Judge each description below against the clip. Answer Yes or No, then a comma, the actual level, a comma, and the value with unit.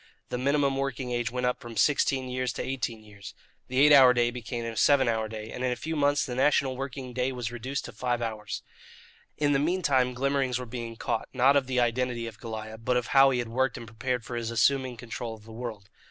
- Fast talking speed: Yes, fast, 235 wpm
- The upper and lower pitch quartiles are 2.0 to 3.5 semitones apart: Yes, narrow, 2.5 semitones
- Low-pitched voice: Yes, low, 125 Hz